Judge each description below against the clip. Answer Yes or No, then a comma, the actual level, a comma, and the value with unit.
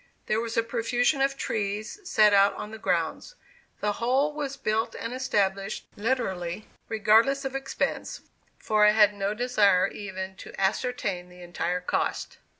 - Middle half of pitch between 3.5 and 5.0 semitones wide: Yes, average, 4.0 semitones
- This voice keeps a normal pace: Yes, average, 150 wpm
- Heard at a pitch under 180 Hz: No, high, 215 Hz